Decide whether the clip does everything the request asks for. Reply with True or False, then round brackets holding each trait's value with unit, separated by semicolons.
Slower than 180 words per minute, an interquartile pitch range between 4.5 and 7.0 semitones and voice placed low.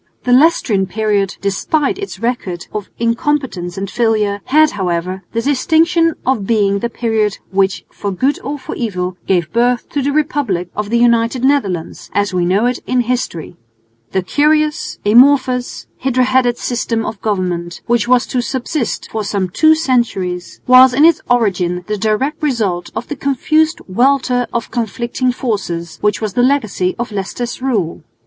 False (160 wpm; 4.9 semitones; 235 Hz)